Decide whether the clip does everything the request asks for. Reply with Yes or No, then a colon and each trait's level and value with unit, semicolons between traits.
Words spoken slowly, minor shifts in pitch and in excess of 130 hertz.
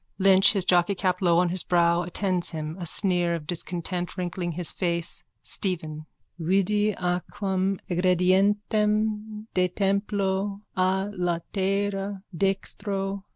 Yes: slow, 110 wpm; narrow, 2.1 semitones; medium, 185 Hz